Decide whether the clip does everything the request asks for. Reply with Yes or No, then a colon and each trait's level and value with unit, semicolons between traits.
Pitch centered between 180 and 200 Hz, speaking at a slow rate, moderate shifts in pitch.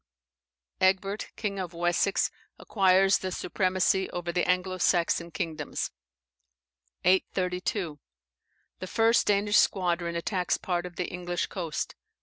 No: medium, 185 Hz; slow, 115 wpm; narrow, 1.8 semitones